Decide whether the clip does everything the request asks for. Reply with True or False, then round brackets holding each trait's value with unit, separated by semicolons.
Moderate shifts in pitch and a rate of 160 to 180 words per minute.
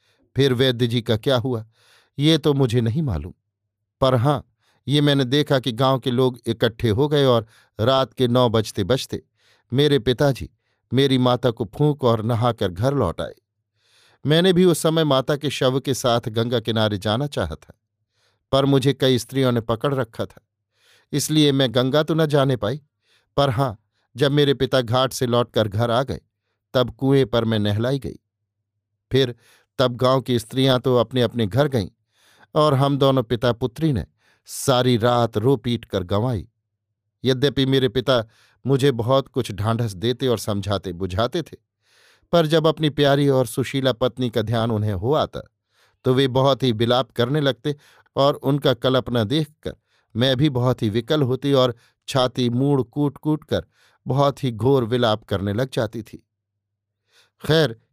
True (3.4 semitones; 170 wpm)